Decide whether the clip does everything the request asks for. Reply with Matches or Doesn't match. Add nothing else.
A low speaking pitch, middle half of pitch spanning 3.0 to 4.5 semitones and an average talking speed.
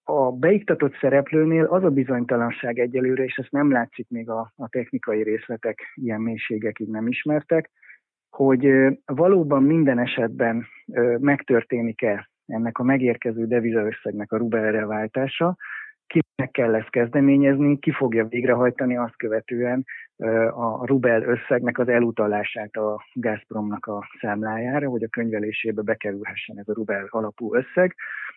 Matches